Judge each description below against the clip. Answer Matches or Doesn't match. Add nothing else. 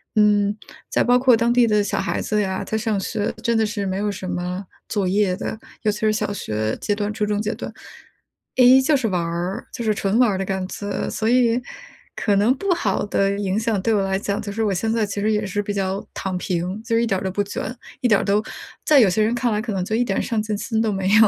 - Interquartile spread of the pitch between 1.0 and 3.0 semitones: Matches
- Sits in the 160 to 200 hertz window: Doesn't match